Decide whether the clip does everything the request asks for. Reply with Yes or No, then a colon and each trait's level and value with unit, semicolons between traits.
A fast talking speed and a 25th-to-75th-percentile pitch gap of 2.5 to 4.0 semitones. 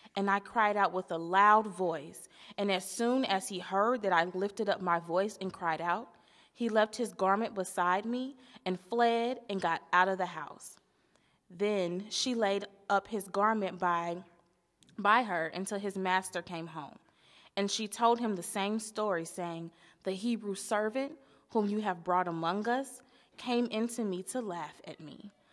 No: average, 175 wpm; average, 3.2 semitones